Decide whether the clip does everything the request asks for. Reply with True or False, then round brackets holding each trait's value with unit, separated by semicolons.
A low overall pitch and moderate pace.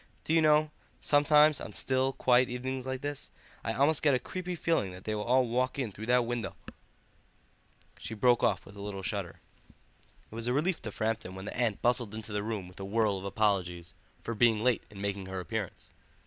False (115 Hz; 210 wpm)